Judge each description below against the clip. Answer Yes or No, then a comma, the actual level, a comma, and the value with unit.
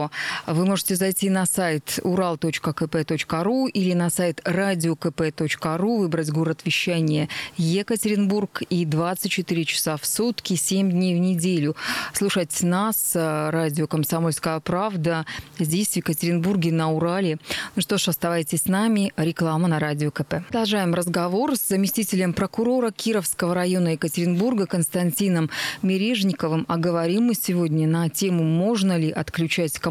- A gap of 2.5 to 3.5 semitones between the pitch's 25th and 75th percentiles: Yes, average, 3.1 semitones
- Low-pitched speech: No, medium, 175 Hz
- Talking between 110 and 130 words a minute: Yes, average, 125 wpm